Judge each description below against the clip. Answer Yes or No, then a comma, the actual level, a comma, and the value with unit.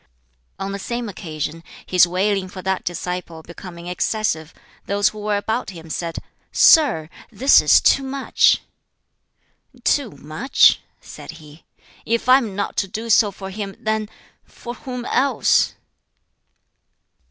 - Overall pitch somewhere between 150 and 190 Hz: No, high, 200 Hz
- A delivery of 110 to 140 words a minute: Yes, slow, 135 wpm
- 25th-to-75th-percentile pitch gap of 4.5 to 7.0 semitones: Yes, average, 4.8 semitones